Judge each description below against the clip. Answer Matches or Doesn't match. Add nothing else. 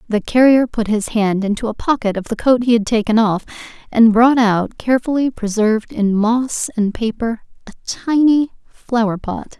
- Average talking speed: Matches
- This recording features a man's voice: Doesn't match